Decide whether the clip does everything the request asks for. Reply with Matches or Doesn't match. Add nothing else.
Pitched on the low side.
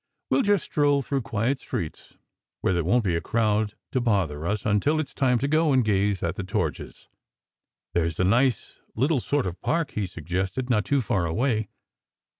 Matches